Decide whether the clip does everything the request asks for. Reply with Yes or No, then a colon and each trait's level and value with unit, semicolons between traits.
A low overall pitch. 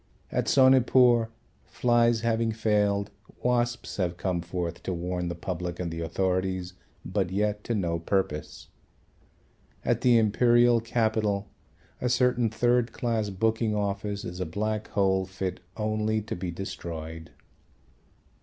Yes: low, 105 Hz